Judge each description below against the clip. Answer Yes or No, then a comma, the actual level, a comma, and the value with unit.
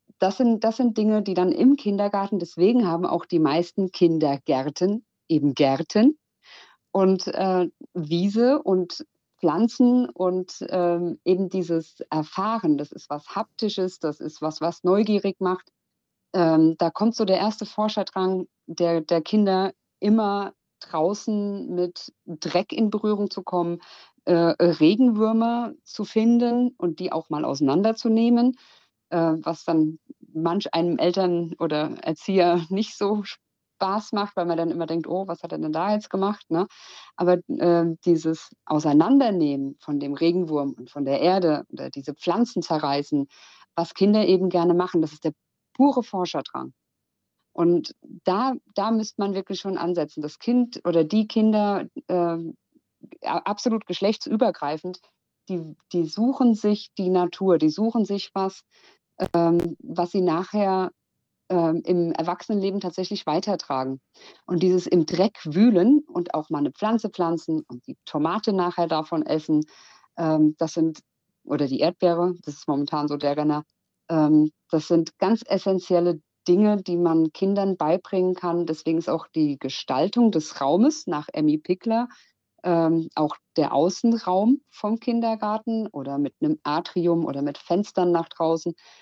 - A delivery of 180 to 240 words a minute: No, average, 145 wpm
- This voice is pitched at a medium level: Yes, medium, 180 Hz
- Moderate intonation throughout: Yes, average, 4.1 semitones